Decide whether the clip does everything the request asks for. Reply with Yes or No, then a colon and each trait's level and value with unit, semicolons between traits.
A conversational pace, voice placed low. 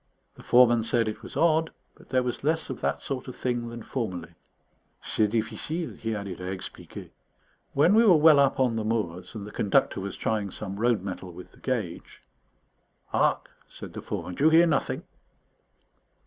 Yes: average, 185 wpm; low, 115 Hz